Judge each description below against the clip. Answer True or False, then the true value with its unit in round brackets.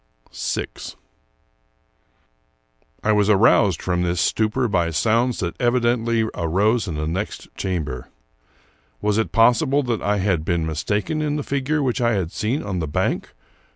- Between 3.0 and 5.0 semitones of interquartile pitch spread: False (5.4 semitones)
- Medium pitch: False (105 Hz)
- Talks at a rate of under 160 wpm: True (150 wpm)